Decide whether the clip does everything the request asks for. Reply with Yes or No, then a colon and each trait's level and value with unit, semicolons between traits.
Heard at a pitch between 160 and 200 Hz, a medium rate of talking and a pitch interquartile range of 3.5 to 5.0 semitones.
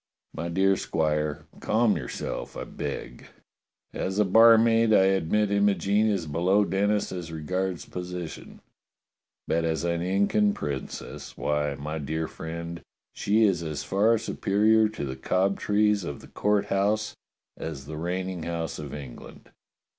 No: very low, 95 Hz; average, 145 wpm; average, 4.3 semitones